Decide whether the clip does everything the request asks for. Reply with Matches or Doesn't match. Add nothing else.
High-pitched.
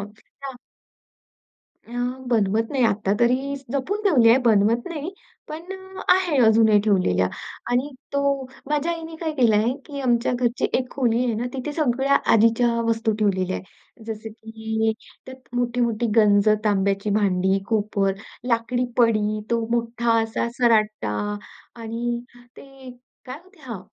Matches